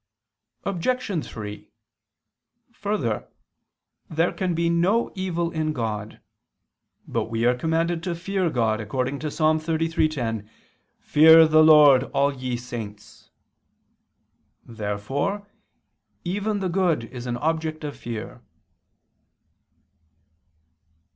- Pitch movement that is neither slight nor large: No, wide, 5.9 semitones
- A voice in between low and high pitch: Yes, medium, 155 Hz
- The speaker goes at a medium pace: No, slow, 100 wpm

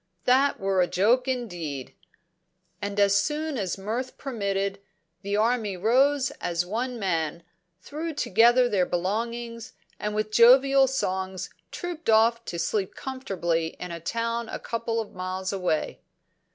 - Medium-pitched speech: No, high, 215 Hz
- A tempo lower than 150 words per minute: Yes, average, 140 wpm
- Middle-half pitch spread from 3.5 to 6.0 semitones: Yes, average, 4.8 semitones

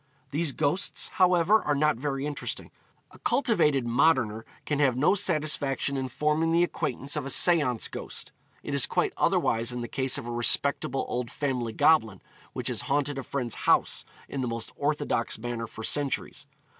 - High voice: No, medium, 140 Hz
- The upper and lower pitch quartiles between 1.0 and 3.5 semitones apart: No, average, 3.9 semitones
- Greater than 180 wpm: No, average, 170 wpm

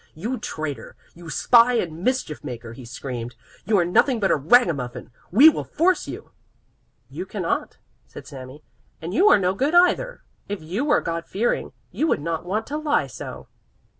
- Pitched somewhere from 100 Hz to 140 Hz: No, medium, 185 Hz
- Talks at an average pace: Yes, average, 175 wpm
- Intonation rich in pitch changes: Yes, wide, 8.9 semitones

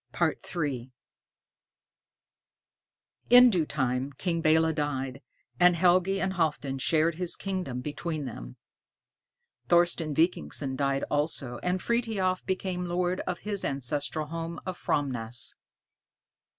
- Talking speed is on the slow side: Yes, slow, 110 wpm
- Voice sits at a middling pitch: Yes, medium, 160 Hz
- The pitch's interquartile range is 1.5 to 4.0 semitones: No, average, 4.8 semitones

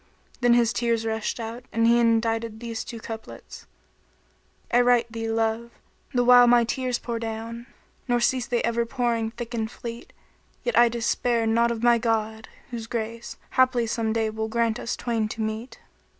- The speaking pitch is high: Yes, high, 230 Hz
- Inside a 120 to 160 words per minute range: No, average, 185 wpm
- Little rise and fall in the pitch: Yes, narrow, 1.1 semitones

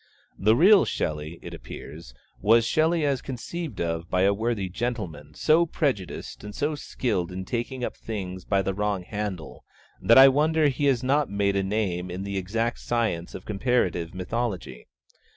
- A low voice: Yes, low, 105 Hz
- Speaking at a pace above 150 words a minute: Yes, average, 170 wpm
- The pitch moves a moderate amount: No, wide, 5.8 semitones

